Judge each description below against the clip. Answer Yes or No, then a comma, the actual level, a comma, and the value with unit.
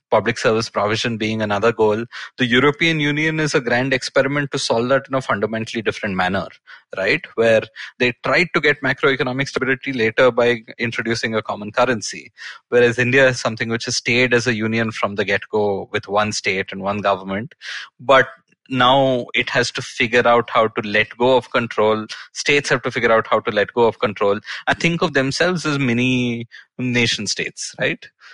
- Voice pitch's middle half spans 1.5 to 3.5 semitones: Yes, average, 3.1 semitones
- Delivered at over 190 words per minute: No, average, 185 wpm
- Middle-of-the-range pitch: No, low, 120 Hz